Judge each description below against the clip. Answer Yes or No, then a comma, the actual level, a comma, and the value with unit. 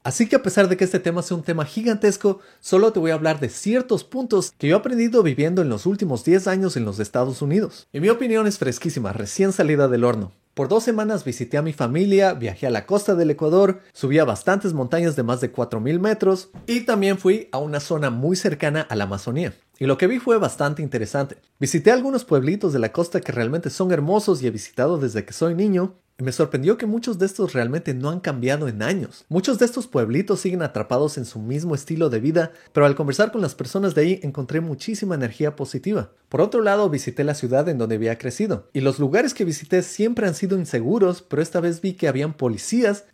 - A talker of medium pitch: Yes, medium, 170 Hz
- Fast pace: Yes, fast, 225 wpm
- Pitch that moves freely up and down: Yes, wide, 6.1 semitones